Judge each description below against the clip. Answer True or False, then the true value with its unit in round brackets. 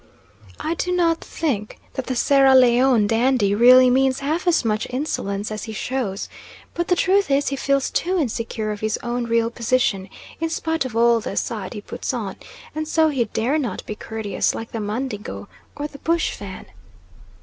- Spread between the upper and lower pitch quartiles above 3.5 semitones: True (4.7 semitones)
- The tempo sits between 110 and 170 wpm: False (185 wpm)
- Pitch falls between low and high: False (250 Hz)